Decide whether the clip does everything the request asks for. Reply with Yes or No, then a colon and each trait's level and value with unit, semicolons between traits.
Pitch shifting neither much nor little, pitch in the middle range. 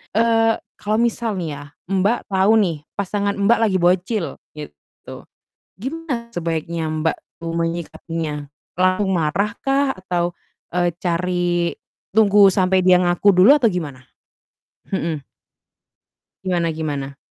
Yes: average, 3.7 semitones; medium, 180 Hz